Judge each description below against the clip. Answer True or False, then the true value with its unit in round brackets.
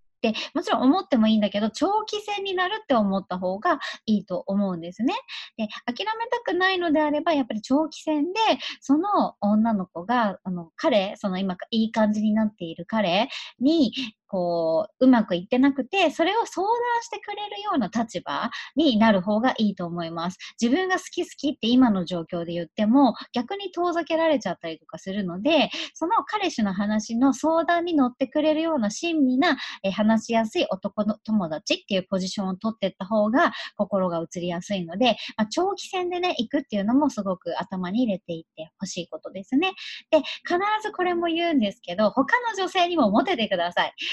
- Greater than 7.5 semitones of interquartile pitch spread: True (8.5 semitones)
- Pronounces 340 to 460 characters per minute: True (375 characters per minute)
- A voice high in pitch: True (245 Hz)